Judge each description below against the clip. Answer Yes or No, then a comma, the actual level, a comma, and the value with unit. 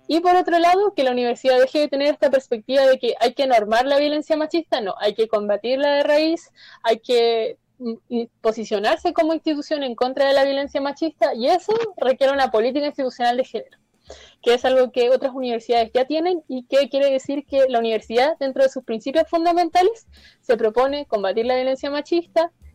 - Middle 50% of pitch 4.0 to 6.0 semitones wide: Yes, average, 4.3 semitones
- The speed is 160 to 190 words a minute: Yes, average, 185 wpm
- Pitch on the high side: Yes, very high, 270 Hz